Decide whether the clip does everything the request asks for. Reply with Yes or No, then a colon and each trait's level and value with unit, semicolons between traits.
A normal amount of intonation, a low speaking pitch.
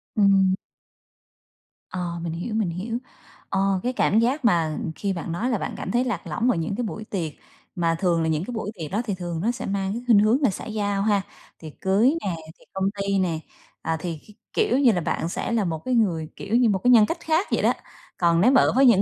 No: average, 5.0 semitones; high, 195 Hz